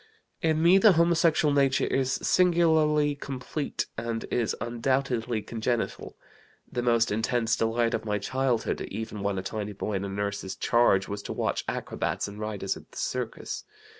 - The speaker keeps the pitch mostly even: No, average, 5.1 semitones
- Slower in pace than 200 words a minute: Yes, average, 160 wpm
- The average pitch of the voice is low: Yes, low, 120 Hz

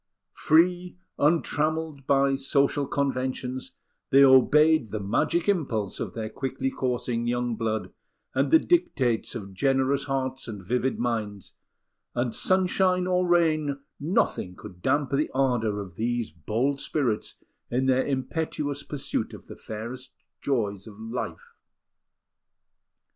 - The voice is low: Yes, low, 130 Hz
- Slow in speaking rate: Yes, slow, 125 wpm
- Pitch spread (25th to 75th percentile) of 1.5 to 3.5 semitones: No, average, 4.4 semitones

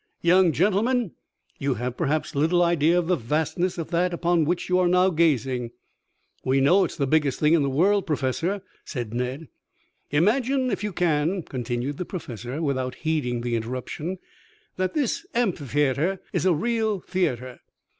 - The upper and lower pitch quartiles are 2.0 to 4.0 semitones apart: No, wide, 5.5 semitones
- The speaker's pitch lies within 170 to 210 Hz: No, medium, 160 Hz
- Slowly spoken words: No, average, 165 wpm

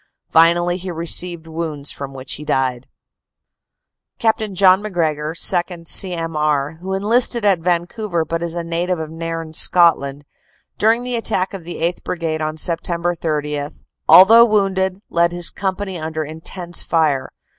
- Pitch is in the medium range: Yes, medium, 170 Hz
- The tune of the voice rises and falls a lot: No, average, 2.8 semitones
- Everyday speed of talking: Yes, average, 155 wpm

